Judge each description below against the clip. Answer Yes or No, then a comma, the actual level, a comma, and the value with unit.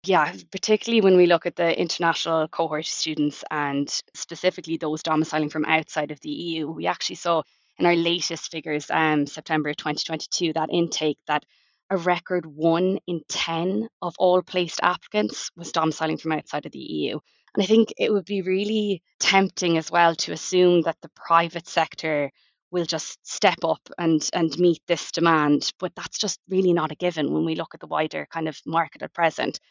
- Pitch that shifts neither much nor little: No, narrow, 2.3 semitones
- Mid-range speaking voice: Yes, medium, 165 Hz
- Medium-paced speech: Yes, average, 190 wpm